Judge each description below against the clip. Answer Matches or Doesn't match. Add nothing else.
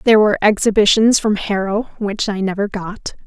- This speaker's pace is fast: Doesn't match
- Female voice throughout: Matches